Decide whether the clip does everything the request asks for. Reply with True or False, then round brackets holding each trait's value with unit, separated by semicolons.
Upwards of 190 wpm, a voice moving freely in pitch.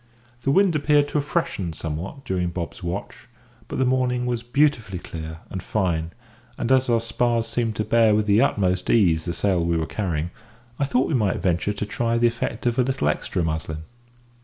True (200 wpm; 6.2 semitones)